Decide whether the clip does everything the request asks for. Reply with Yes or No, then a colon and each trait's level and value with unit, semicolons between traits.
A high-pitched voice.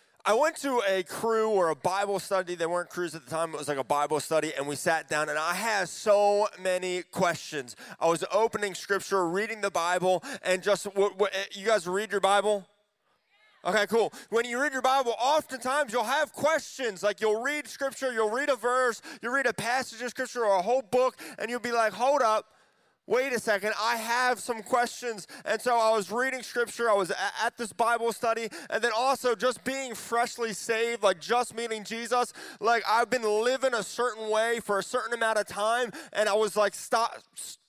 Yes: high, 225 Hz